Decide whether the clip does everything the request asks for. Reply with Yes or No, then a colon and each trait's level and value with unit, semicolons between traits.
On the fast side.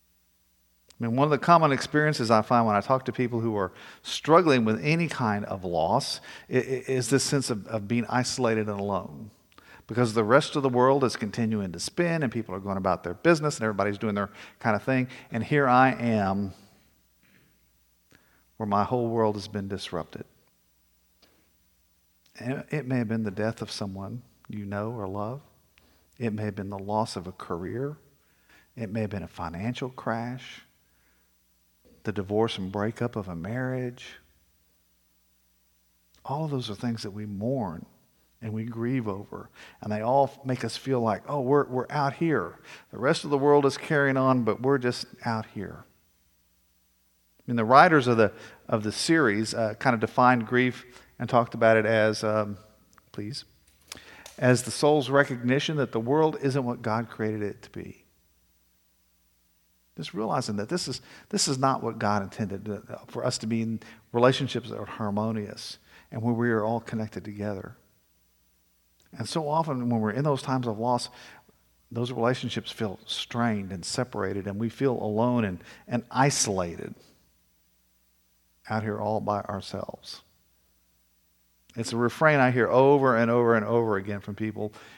No: average, 170 wpm